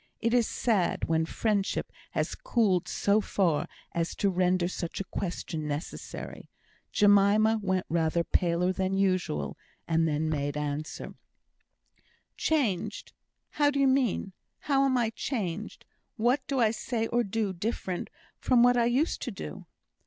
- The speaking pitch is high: Yes, high, 195 Hz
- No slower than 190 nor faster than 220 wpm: No, average, 145 wpm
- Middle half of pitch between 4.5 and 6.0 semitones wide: Yes, wide, 5.4 semitones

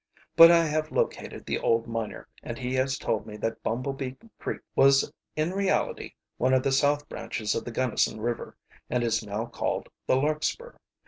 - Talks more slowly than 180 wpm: No, average, 185 wpm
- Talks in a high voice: No, low, 130 Hz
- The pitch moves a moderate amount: Yes, average, 4.3 semitones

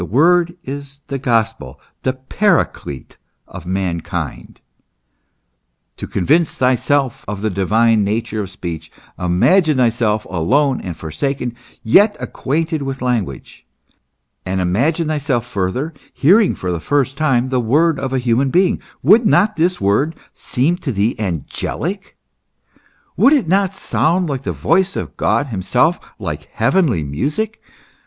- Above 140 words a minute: No, slow, 135 wpm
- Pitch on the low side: Yes, low, 130 Hz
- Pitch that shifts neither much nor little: No, wide, 8.0 semitones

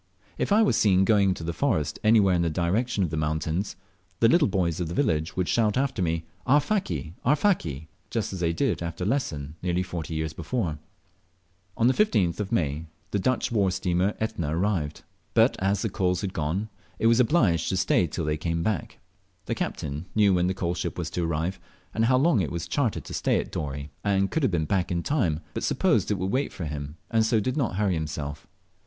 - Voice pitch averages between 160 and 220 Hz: No, very low, 90 Hz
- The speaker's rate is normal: No, fast, 210 wpm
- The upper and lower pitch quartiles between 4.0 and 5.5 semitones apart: Yes, average, 5.2 semitones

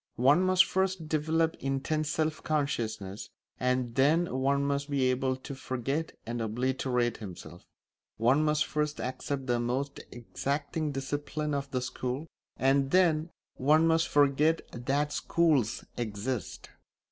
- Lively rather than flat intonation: No, average, 3.2 semitones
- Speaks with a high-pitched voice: No, medium, 140 Hz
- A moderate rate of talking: No, slow, 130 wpm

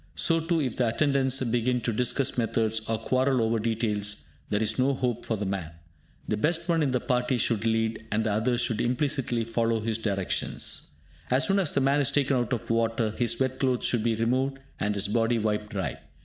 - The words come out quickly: Yes, fast, 210 wpm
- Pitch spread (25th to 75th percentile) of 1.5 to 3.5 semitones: Yes, average, 2.9 semitones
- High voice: No, low, 115 Hz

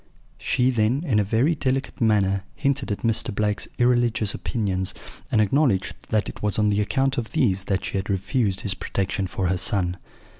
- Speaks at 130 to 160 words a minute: No, average, 185 wpm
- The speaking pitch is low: Yes, low, 105 Hz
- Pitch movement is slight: No, average, 4.2 semitones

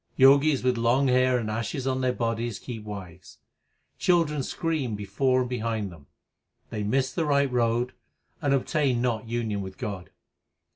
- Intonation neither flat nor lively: Yes, average, 3.7 semitones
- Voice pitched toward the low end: Yes, low, 125 Hz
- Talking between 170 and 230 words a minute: No, average, 160 wpm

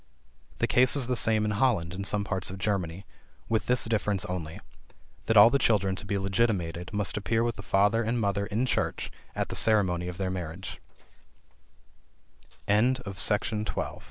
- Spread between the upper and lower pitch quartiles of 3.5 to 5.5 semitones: No, average, 3.0 semitones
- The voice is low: Yes, low, 105 Hz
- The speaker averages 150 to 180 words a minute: Yes, average, 170 wpm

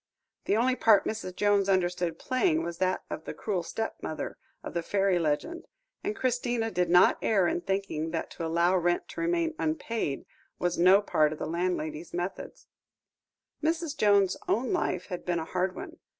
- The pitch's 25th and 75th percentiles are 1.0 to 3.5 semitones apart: No, average, 5.1 semitones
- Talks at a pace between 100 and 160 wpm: No, average, 170 wpm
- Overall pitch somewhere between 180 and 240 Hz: Yes, high, 190 Hz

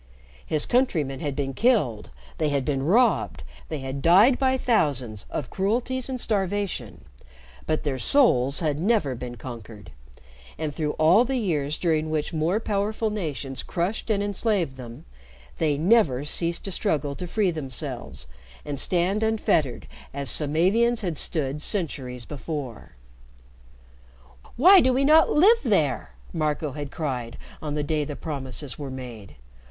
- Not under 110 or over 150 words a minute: Yes, average, 145 wpm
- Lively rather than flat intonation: Yes, wide, 7.1 semitones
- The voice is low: No, medium, 155 Hz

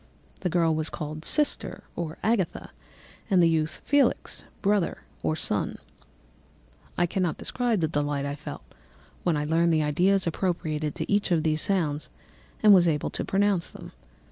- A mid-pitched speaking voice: Yes, medium, 165 Hz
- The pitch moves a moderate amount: Yes, average, 3.9 semitones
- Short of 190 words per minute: Yes, average, 165 wpm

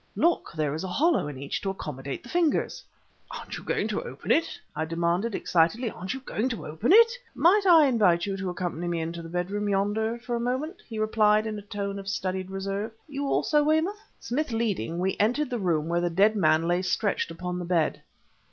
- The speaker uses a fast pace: Yes, fast, 215 wpm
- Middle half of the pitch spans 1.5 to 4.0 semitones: No, wide, 5.6 semitones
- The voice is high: Yes, high, 200 Hz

